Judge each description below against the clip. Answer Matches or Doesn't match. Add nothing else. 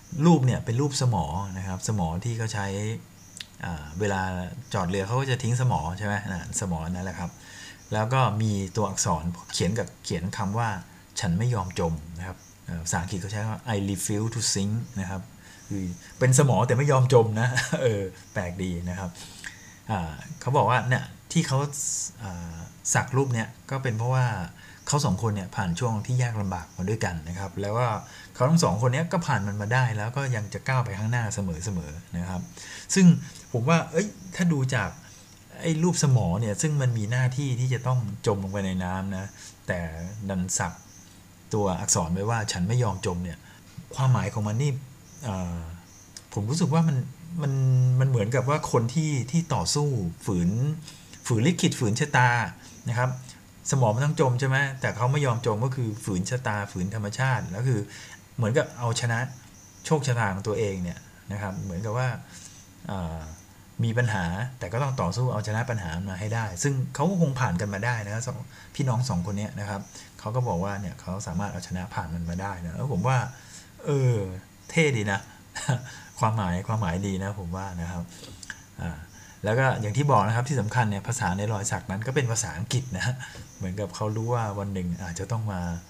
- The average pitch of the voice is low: Matches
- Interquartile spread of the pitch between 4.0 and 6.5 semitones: Matches